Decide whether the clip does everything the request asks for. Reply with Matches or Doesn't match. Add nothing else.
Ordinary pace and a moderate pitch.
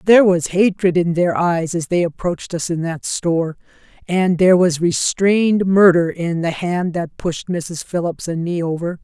Matches